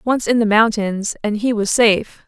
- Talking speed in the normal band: No, fast, 210 wpm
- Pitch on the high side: Yes, high, 220 Hz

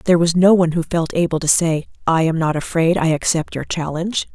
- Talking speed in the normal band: No, fast, 235 wpm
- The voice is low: No, medium, 165 Hz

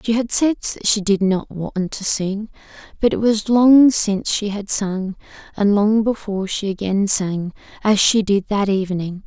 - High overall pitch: Yes, high, 205 Hz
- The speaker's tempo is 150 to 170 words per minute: No, average, 180 wpm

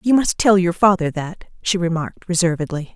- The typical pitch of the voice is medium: Yes, medium, 180 Hz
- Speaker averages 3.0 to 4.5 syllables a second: No, 5.8 syllables/s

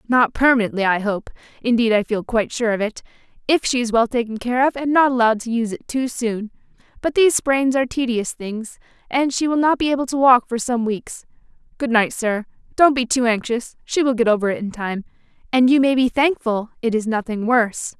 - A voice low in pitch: No, high, 240 Hz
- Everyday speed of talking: No, fast, 220 wpm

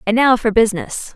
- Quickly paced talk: Yes, fast, 210 wpm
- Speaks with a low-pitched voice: No, high, 225 Hz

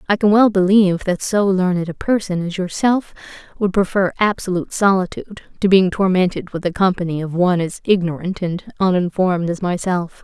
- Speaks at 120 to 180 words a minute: Yes, average, 170 wpm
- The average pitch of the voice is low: No, medium, 185 Hz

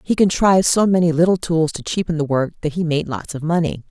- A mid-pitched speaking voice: Yes, medium, 165 Hz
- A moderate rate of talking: No, fast, 245 wpm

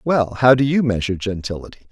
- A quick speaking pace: No, average, 190 wpm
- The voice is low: Yes, low, 115 Hz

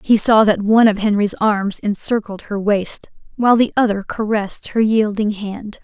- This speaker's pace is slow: No, average, 175 wpm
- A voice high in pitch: Yes, high, 210 Hz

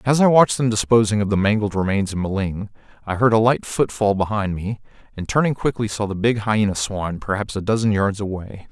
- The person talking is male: Yes, male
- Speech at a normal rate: No, fast, 215 wpm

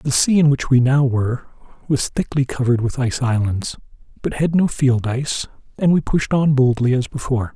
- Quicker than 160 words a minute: Yes, average, 200 wpm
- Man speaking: Yes, male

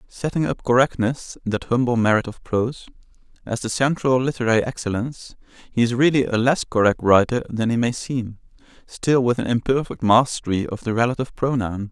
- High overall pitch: No, low, 120 Hz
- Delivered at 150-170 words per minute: Yes, average, 165 wpm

